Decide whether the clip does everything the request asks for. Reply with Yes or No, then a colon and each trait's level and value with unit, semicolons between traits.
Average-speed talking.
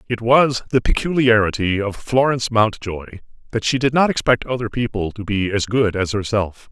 Yes: average, 180 wpm